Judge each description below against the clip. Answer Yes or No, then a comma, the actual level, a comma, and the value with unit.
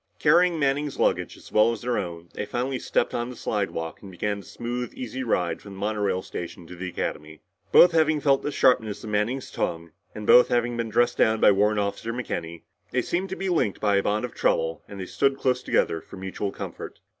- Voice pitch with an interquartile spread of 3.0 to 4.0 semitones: No, average, 4.7 semitones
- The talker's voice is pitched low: Yes, low, 110 Hz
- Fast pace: Yes, fast, 220 wpm